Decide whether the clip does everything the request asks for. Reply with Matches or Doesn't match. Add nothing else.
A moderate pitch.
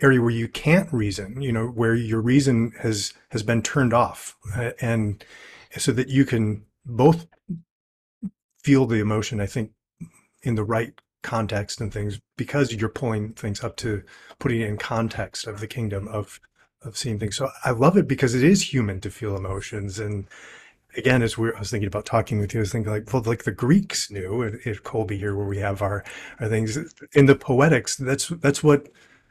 Doesn't match